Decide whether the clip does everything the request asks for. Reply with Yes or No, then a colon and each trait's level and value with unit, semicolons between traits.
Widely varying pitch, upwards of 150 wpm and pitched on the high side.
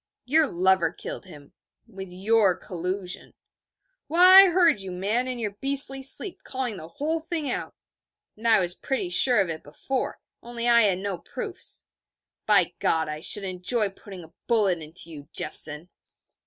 Yes: wide, 6.2 semitones; average, 165 wpm; high, 200 Hz